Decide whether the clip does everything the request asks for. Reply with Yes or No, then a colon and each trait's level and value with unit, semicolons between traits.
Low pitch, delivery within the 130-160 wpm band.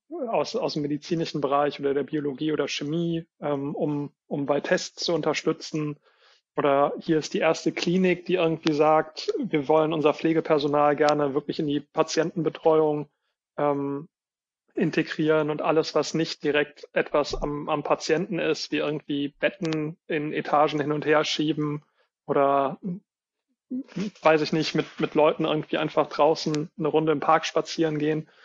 No: medium, 155 Hz; average, 150 wpm